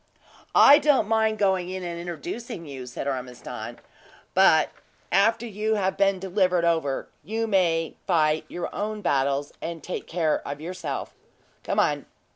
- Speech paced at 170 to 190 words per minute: No, average, 145 wpm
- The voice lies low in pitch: No, medium, 180 Hz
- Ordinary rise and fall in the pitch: Yes, average, 4.9 semitones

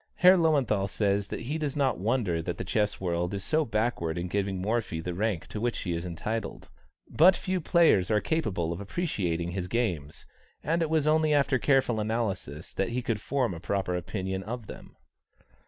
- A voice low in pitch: Yes, low, 105 Hz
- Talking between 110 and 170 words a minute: No, average, 190 wpm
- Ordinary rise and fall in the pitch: No, wide, 6.9 semitones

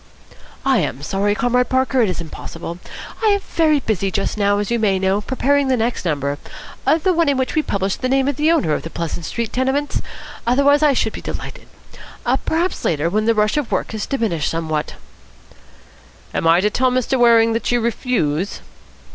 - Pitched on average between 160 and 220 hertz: No, high, 230 Hz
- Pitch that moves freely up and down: Yes, wide, 5.8 semitones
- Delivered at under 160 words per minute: No, average, 195 wpm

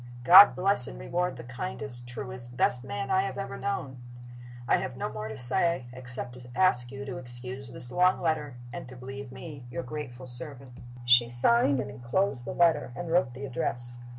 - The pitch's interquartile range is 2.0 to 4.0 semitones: No, average, 4.4 semitones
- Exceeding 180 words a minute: Yes, average, 195 wpm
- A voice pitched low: Yes, low, 130 Hz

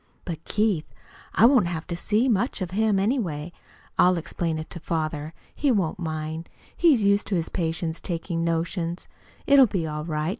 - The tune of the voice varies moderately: Yes, average, 4.2 semitones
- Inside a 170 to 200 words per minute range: Yes, average, 175 wpm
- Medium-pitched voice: Yes, medium, 170 Hz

